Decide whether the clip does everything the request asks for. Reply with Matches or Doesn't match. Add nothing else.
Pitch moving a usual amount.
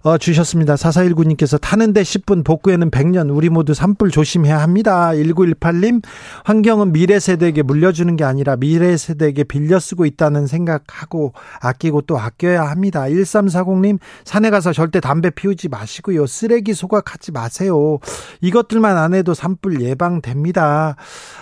Matches